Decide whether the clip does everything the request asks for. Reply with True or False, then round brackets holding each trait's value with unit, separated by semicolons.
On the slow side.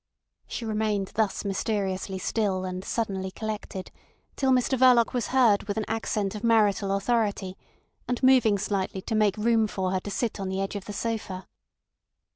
False (170 wpm)